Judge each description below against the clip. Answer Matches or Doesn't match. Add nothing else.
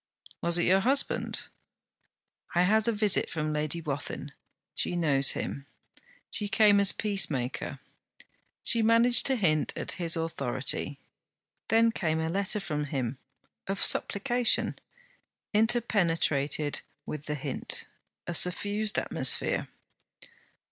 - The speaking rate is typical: Doesn't match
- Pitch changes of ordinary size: Doesn't match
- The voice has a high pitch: Doesn't match